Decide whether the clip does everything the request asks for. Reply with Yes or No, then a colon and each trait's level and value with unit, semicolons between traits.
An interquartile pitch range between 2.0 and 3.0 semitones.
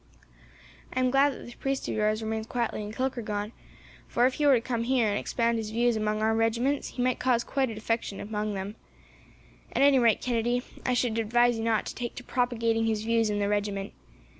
Yes: narrow, 2.4 semitones